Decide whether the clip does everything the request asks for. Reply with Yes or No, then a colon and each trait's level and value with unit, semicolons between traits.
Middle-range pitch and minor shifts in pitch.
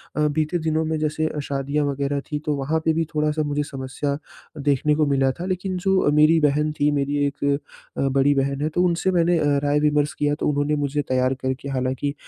Yes: medium, 150 Hz; narrow, 1.9 semitones